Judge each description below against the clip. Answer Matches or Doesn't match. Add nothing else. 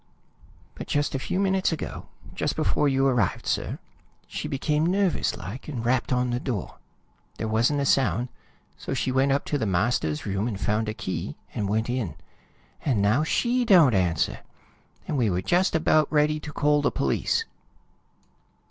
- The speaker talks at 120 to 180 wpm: Matches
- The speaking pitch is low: Matches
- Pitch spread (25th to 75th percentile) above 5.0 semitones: Matches